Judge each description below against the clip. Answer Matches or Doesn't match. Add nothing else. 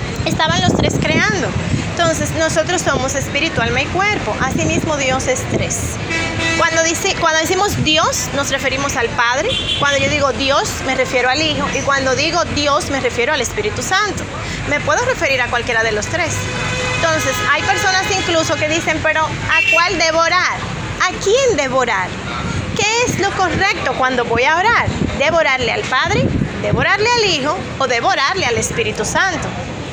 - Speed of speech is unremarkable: Matches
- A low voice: Doesn't match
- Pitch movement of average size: Doesn't match